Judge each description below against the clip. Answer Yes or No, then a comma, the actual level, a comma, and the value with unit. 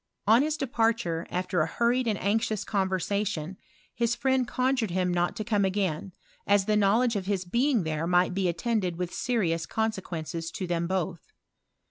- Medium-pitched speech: No, high, 195 Hz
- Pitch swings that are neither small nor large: Yes, average, 4.4 semitones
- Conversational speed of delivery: Yes, average, 175 wpm